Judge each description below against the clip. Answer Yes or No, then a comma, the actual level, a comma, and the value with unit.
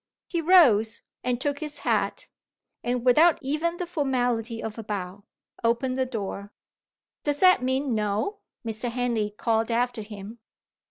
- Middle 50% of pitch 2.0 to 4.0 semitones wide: No, average, 4.5 semitones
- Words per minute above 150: No, average, 145 wpm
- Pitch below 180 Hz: No, high, 245 Hz